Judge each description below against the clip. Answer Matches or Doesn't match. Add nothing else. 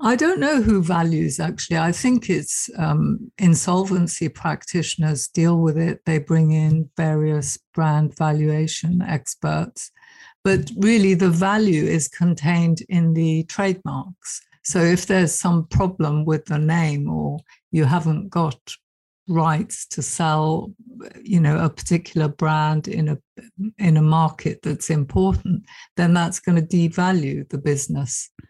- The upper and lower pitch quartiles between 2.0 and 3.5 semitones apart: Matches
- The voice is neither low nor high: Matches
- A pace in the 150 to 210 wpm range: Doesn't match